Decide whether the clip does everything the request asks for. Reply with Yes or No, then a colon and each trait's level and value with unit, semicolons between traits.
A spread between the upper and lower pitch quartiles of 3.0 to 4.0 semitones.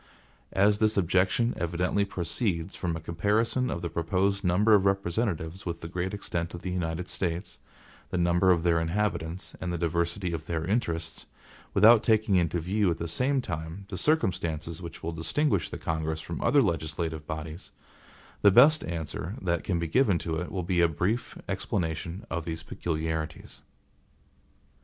Yes: average, 3.3 semitones